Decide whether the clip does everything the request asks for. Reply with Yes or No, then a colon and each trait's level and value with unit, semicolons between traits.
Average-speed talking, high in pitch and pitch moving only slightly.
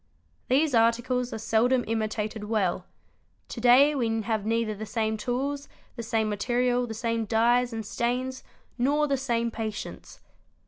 Yes: average, 145 wpm; high, 230 Hz; narrow, 2.2 semitones